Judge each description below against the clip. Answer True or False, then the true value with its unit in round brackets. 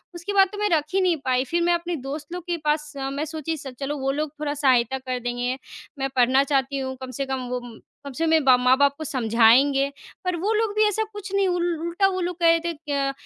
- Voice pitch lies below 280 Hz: False (290 Hz)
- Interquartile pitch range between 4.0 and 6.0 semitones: True (4.6 semitones)